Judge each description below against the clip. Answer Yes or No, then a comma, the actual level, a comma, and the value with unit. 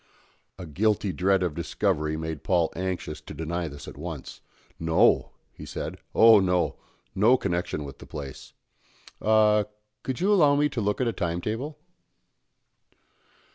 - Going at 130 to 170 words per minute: Yes, average, 150 wpm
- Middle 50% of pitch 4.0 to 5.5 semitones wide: Yes, average, 5.1 semitones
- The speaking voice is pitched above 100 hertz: No, very low, 90 Hz